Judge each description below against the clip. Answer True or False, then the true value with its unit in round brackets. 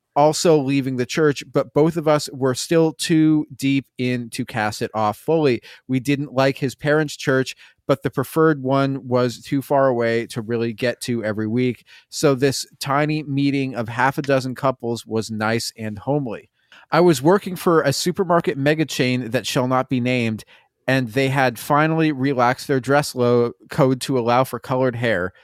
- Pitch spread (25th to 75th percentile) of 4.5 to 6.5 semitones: False (3.2 semitones)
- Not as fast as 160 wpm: False (180 wpm)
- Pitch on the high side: False (135 Hz)